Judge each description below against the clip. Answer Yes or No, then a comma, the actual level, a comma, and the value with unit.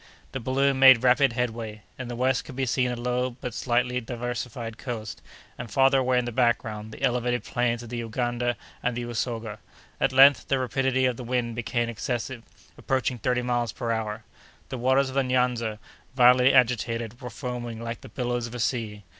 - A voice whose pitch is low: Yes, low, 120 Hz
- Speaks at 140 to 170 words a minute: No, average, 195 wpm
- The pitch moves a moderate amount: No, narrow, 1.6 semitones